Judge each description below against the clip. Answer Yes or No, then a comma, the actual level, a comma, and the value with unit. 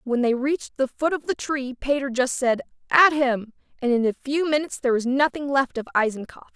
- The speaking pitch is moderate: No, very high, 265 Hz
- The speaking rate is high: Yes, fast, 220 wpm